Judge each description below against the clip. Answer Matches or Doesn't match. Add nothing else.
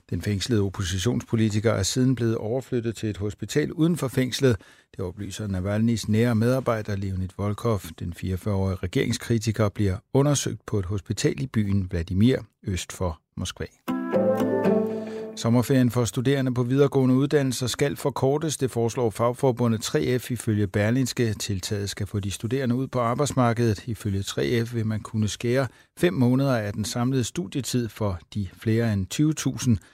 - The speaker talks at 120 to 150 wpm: Matches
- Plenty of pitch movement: Doesn't match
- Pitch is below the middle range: Matches